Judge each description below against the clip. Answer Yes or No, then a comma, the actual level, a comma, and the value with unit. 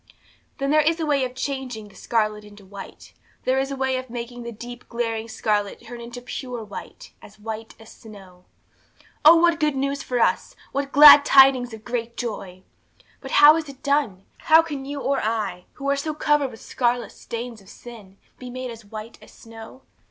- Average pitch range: Yes, average, 3.9 semitones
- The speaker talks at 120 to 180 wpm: No, average, 195 wpm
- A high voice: Yes, high, 245 Hz